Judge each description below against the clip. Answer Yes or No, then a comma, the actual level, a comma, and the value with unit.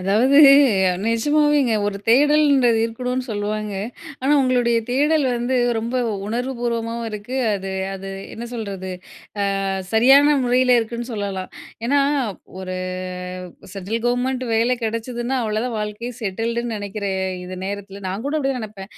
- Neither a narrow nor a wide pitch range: Yes, average, 3.4 semitones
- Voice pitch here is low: No, high, 230 Hz